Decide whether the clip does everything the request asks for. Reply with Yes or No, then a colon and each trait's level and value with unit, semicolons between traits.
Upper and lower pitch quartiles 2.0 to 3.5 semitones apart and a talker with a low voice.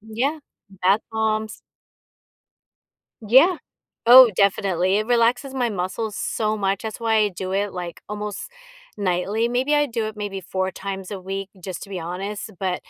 No: average, 2.8 semitones; high, 210 Hz